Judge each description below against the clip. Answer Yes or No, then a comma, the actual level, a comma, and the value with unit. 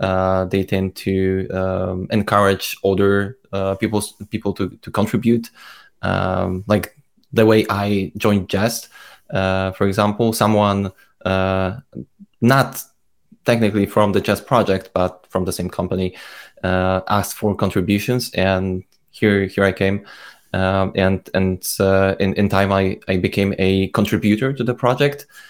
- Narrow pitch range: Yes, narrow, 1.9 semitones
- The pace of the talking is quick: No, average, 140 wpm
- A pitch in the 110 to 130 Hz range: No, low, 100 Hz